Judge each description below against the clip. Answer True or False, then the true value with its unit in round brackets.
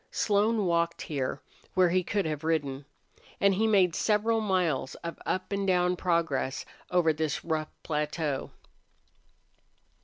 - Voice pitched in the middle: True (170 Hz)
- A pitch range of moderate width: True (4.0 semitones)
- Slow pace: True (130 wpm)